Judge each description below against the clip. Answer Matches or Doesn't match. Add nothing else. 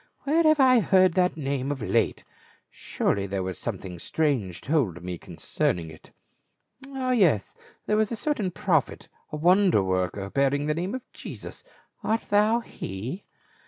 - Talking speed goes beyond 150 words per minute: Matches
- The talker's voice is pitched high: Doesn't match